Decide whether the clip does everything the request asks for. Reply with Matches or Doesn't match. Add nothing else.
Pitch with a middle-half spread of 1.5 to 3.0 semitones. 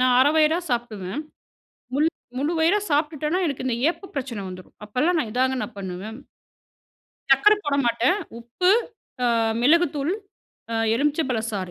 Doesn't match